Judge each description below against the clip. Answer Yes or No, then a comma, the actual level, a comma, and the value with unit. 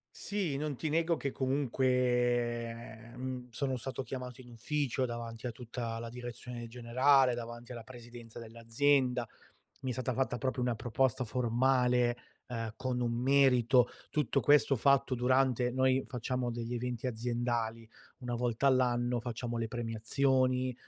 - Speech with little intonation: Yes, narrow, 1.8 semitones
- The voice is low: Yes, low, 125 Hz